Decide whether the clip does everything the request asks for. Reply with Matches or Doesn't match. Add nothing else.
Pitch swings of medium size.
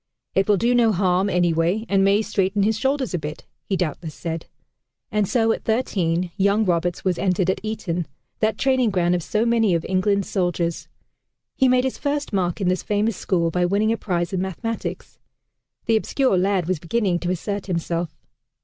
Matches